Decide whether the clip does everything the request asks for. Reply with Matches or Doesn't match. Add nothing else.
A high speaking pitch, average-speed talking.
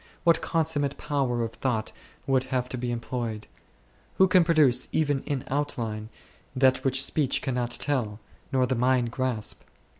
Doesn't match